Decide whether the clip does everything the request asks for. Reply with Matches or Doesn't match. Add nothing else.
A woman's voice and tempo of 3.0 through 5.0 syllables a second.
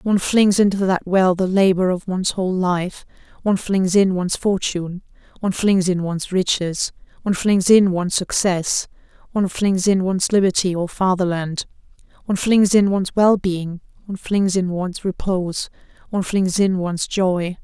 Doesn't match